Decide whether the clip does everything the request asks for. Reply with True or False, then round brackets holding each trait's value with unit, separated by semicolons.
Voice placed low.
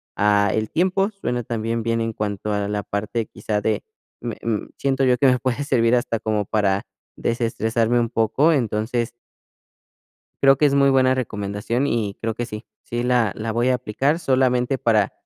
True (115 Hz)